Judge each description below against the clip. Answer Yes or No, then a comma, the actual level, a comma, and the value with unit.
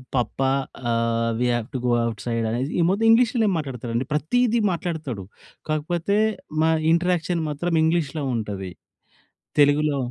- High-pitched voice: No, medium, 150 Hz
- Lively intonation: Yes, wide, 6.4 semitones